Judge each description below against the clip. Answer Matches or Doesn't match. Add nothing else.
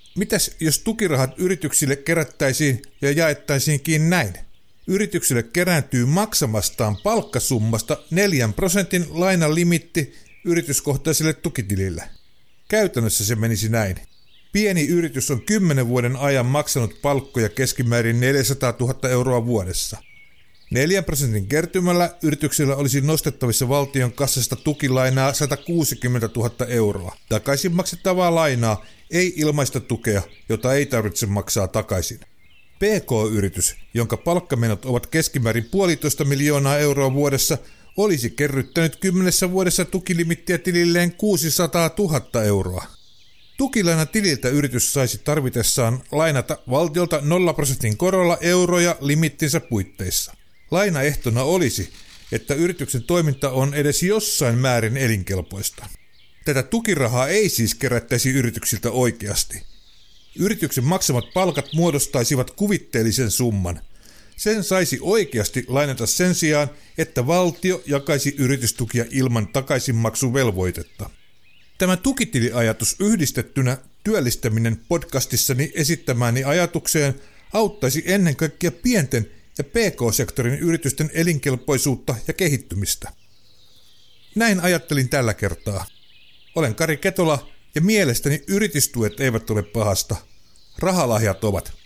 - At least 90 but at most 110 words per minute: Matches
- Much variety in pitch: Matches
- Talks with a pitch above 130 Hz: Matches